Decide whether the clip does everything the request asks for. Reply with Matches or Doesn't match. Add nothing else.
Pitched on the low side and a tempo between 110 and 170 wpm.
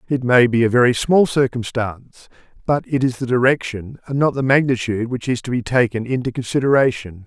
Doesn't match